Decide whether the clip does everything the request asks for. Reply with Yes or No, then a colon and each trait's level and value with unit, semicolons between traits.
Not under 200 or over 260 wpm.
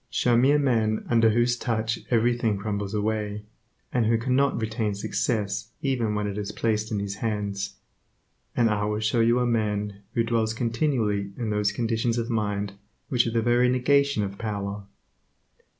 No: average, 170 wpm